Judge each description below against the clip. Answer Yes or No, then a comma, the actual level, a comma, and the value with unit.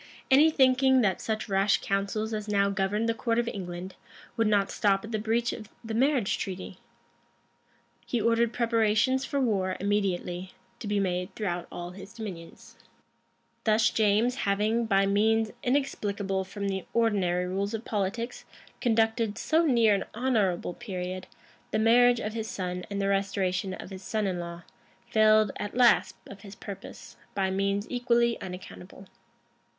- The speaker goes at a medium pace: Yes, average, 155 wpm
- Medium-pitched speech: No, high, 210 Hz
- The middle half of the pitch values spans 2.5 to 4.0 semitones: Yes, average, 3.0 semitones